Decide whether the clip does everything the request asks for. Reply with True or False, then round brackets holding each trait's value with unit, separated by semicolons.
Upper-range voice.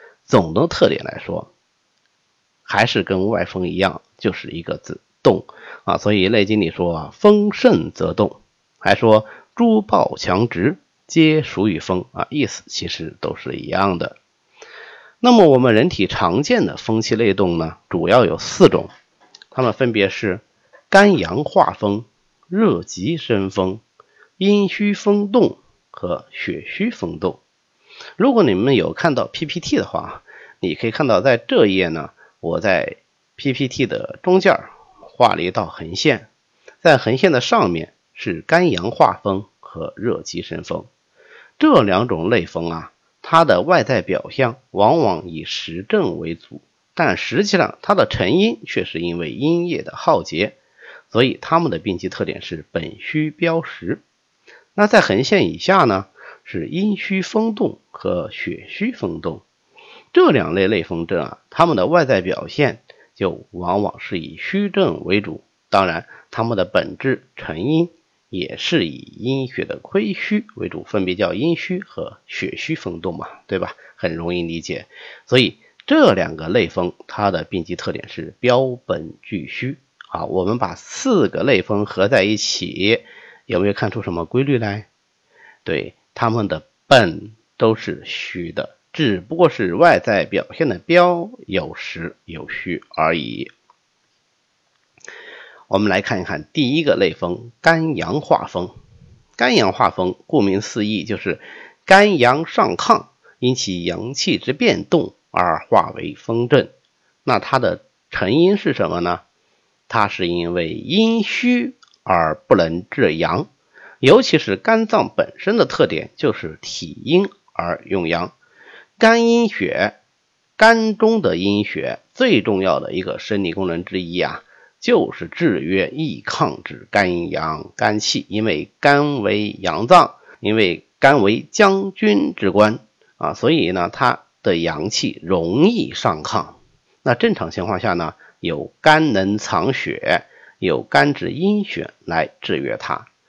False (135 Hz)